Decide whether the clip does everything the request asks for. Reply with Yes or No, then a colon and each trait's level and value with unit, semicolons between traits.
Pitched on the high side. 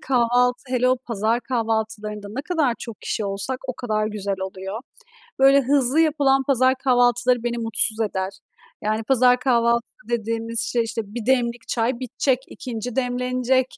Yes: high, 240 Hz